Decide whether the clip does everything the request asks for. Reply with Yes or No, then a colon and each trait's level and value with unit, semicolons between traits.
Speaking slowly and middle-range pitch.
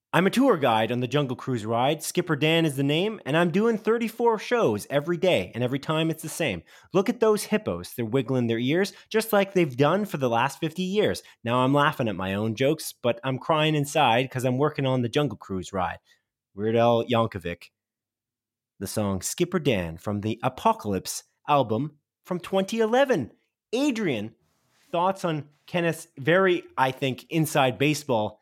No: average, 180 wpm; medium, 145 Hz